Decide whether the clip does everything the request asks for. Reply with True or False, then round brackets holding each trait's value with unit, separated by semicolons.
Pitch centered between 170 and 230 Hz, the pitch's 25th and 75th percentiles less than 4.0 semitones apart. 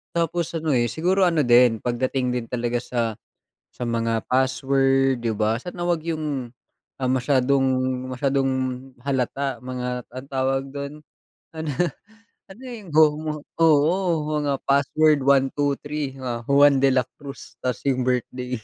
False (135 Hz; 3.3 semitones)